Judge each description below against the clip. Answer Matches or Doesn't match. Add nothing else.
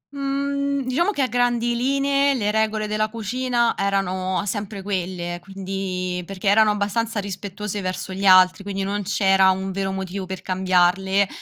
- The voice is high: Matches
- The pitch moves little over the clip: Doesn't match